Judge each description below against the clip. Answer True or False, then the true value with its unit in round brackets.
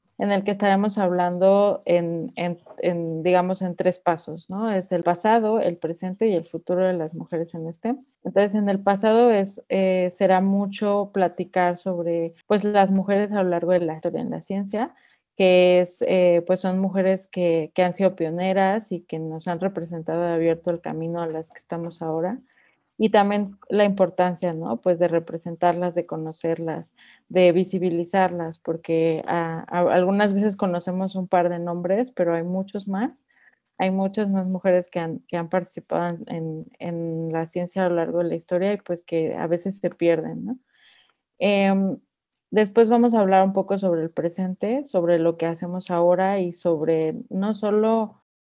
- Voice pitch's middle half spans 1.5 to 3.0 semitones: True (2.5 semitones)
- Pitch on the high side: False (180 Hz)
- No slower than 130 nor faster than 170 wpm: False (180 wpm)